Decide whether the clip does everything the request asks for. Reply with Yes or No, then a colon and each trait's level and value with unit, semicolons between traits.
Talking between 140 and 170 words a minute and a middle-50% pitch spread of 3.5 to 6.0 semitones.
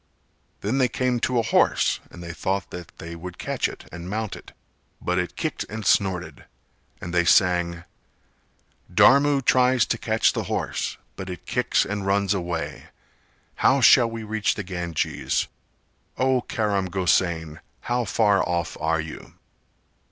Yes: average, 150 wpm; average, 4.7 semitones